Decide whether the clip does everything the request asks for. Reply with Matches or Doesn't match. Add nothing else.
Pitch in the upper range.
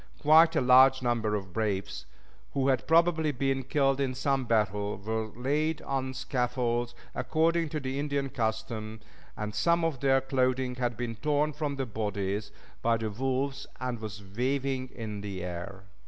Doesn't match